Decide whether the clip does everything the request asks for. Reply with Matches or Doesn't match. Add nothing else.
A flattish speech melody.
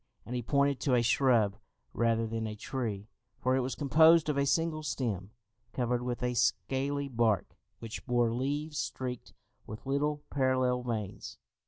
Doesn't match